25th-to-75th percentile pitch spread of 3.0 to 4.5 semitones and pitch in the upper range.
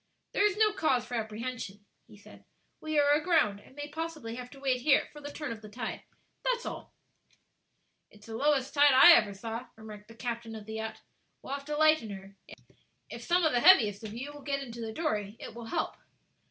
No: average, 5.1 semitones; very high, 250 Hz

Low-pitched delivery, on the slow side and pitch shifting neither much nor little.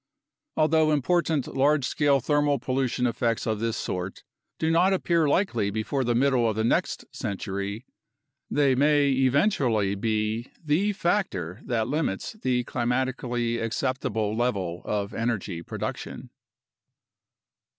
Yes: low, 125 Hz; slow, 120 wpm; average, 4.9 semitones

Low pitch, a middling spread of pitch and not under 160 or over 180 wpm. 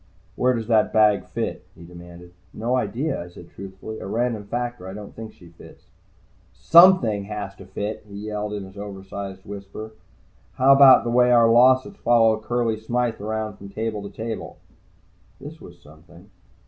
Yes: low, 110 Hz; average, 3.4 semitones; average, 170 wpm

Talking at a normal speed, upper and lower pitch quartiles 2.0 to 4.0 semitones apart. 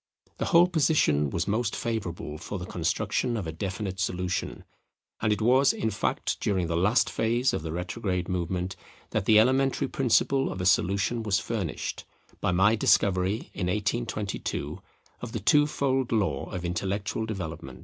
No: average, 160 wpm; average, 4.4 semitones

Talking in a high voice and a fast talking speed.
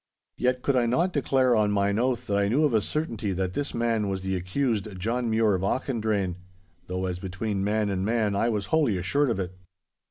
No: low, 110 Hz; fast, 215 wpm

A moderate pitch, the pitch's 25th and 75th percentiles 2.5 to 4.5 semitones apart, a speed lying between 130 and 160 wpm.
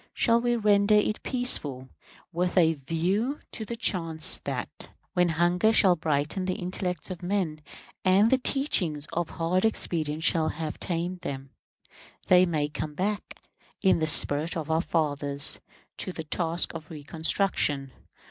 Yes: medium, 175 Hz; average, 3.9 semitones; average, 150 wpm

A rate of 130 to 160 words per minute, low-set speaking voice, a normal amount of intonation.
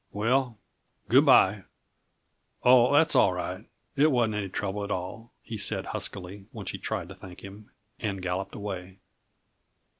Yes: average, 150 wpm; low, 105 Hz; average, 3.9 semitones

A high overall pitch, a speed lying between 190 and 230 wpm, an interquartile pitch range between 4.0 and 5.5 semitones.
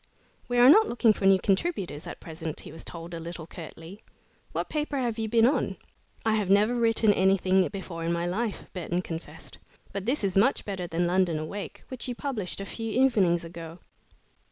Yes: high, 195 Hz; average, 195 wpm; average, 5.0 semitones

